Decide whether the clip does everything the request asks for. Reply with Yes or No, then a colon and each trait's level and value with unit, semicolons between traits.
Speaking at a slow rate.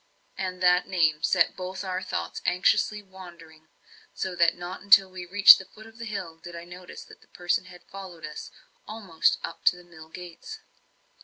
No: average, 180 wpm